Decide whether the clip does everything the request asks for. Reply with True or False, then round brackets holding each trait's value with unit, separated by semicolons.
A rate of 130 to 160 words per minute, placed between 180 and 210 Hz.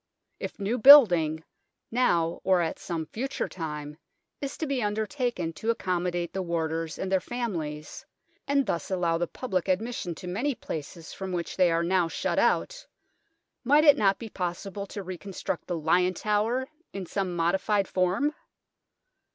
True (155 wpm; 185 Hz)